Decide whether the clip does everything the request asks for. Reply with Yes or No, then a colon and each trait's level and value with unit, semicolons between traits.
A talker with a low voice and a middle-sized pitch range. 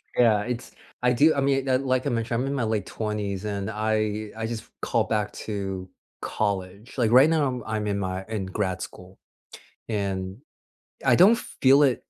Yes: low, 110 Hz; average, 4.0 semitones